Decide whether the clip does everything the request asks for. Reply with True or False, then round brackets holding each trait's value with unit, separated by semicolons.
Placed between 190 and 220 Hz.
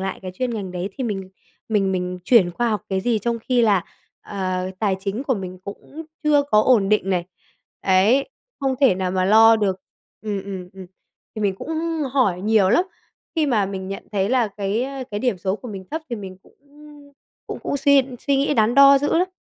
True (210 Hz)